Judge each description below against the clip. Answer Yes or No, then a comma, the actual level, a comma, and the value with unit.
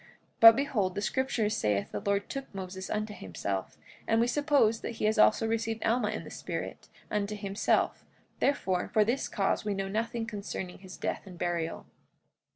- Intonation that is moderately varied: Yes, average, 3.1 semitones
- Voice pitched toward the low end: No, high, 210 Hz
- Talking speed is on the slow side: No, average, 175 wpm